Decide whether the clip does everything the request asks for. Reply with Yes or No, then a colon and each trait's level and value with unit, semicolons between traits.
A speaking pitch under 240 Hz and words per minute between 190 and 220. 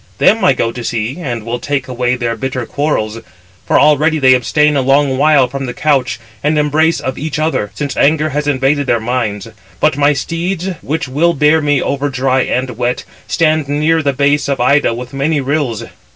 Yes: medium, 140 Hz; average, 195 wpm